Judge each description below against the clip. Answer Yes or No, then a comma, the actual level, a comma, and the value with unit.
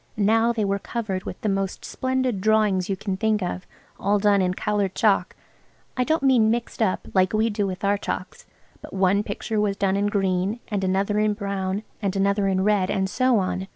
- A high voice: Yes, high, 200 Hz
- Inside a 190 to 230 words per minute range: Yes, average, 195 wpm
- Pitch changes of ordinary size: No, narrow, 2.1 semitones